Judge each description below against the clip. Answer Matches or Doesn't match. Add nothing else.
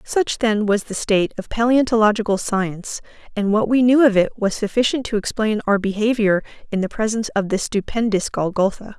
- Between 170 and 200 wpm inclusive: Matches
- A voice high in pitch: Matches